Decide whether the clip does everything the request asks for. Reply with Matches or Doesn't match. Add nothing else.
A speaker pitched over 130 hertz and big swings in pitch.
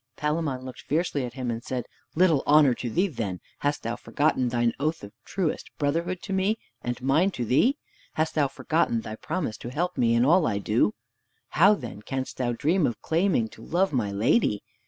Matches